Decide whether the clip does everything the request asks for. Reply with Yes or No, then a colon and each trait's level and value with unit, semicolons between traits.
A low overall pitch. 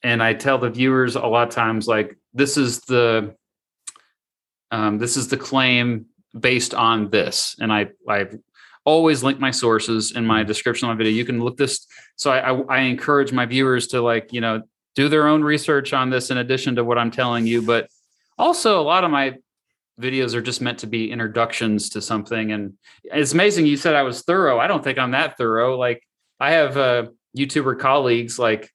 Yes: low, 120 Hz